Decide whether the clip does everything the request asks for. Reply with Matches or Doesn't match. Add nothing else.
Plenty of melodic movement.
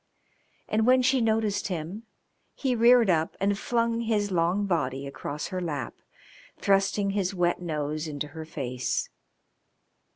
Matches